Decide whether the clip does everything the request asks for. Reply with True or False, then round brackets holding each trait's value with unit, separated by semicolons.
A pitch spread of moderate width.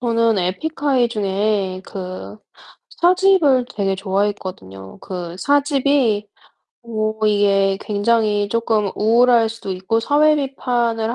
True (4.0 semitones)